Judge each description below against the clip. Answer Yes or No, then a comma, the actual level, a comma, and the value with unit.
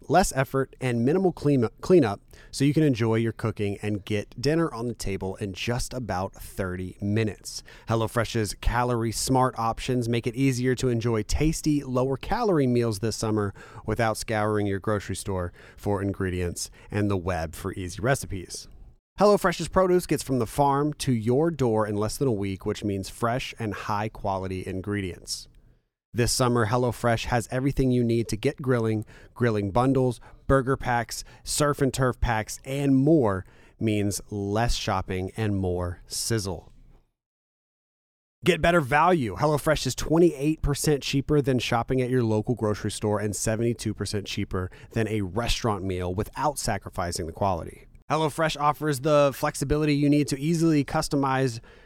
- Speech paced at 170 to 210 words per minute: No, average, 155 wpm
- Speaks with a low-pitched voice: Yes, low, 115 Hz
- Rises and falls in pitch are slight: No, average, 4.8 semitones